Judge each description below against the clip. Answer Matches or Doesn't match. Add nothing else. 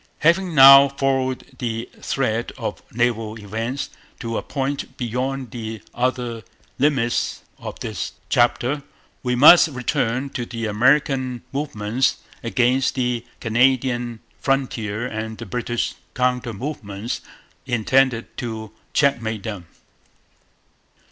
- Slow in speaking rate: Matches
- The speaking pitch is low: Matches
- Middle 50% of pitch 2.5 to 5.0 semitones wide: Matches